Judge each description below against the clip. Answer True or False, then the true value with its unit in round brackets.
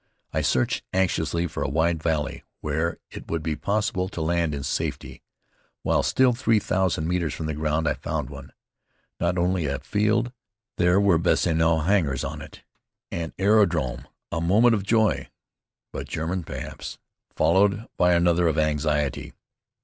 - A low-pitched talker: True (85 Hz)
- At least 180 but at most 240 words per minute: False (155 wpm)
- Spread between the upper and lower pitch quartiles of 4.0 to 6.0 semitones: False (3.4 semitones)